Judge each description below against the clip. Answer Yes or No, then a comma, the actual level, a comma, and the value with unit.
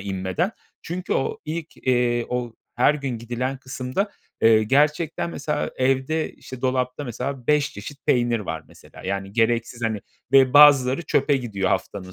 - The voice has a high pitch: No, low, 125 Hz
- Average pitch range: Yes, average, 3.9 semitones